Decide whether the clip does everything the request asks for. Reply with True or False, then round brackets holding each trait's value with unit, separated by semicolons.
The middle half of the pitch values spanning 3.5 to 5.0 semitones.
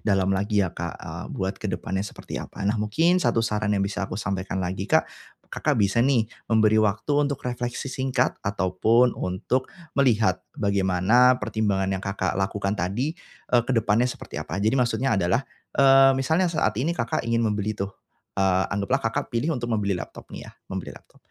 True (4.2 semitones)